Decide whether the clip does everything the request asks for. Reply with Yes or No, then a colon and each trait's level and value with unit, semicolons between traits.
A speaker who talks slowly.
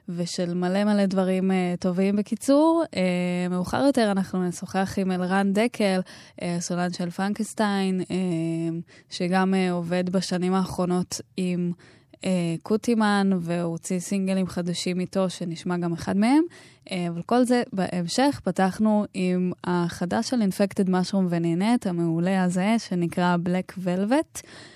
No: average, 125 wpm